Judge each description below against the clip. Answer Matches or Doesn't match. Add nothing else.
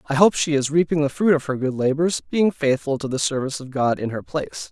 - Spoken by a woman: Doesn't match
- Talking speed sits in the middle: Doesn't match